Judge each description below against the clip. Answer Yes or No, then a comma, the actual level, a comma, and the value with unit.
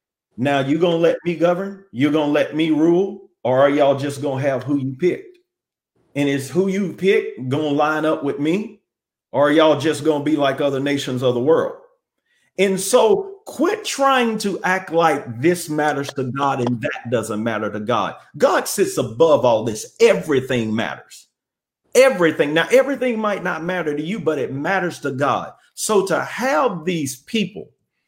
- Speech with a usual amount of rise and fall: No, wide, 6.3 semitones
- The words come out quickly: No, average, 190 wpm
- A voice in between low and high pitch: Yes, medium, 160 Hz